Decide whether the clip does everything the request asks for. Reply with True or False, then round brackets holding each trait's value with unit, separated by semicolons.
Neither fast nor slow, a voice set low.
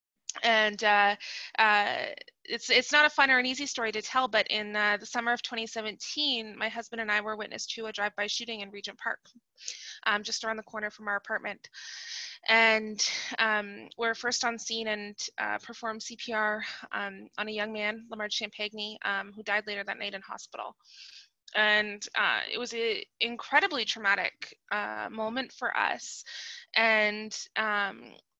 False (170 wpm; 220 Hz)